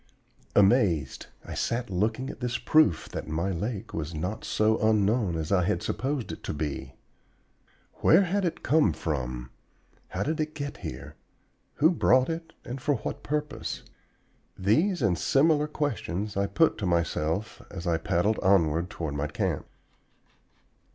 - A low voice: Yes, low, 105 Hz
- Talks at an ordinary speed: Yes, average, 150 wpm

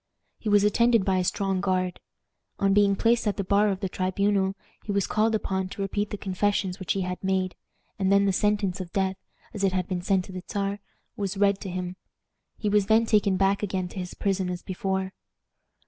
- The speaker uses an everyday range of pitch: No, narrow, 1.6 semitones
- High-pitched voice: Yes, high, 195 Hz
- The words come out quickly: Yes, fast, 215 wpm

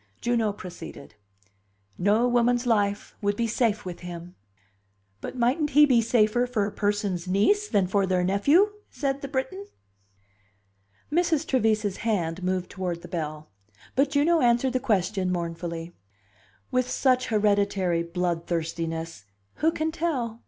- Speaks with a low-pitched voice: No, high, 210 Hz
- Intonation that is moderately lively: No, wide, 5.8 semitones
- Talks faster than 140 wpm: No, slow, 135 wpm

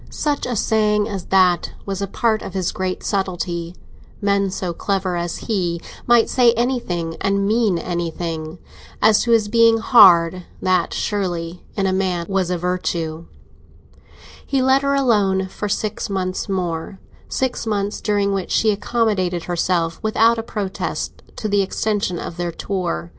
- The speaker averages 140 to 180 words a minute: Yes, average, 155 wpm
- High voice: Yes, high, 195 Hz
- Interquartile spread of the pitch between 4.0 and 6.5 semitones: No, average, 3.6 semitones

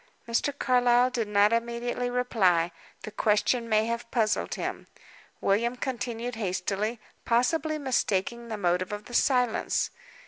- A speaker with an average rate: No, slow, 130 wpm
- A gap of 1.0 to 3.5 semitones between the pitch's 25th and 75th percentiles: Yes, average, 2.8 semitones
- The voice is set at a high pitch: Yes, high, 235 Hz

